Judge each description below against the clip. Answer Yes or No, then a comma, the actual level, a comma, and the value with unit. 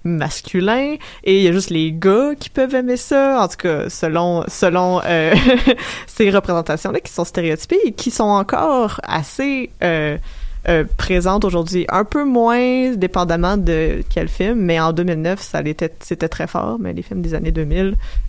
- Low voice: No, medium, 185 Hz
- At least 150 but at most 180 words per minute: Yes, average, 175 wpm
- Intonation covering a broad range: Yes, wide, 6.1 semitones